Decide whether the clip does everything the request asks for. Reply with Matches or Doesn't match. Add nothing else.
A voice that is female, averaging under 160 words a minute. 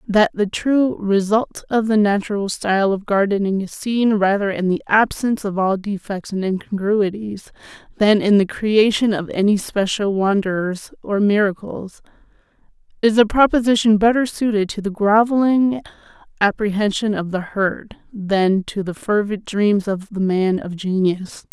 Matches